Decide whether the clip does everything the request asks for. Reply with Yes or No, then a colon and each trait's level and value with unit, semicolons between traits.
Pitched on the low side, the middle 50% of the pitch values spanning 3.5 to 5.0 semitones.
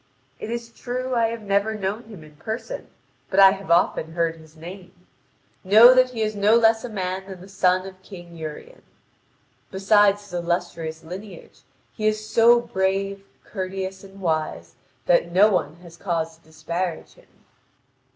No: high, 190 Hz; average, 3.9 semitones